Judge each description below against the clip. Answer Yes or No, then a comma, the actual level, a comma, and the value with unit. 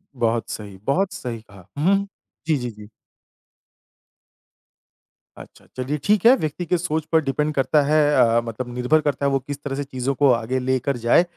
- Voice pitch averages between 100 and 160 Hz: Yes, low, 135 Hz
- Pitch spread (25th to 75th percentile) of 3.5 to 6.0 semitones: Yes, average, 4.3 semitones